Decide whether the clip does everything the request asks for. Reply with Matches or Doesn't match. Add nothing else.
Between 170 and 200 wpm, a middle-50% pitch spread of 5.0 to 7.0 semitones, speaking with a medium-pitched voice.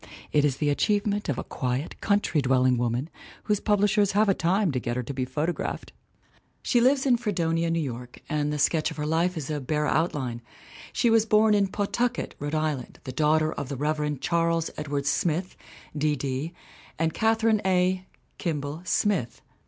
Matches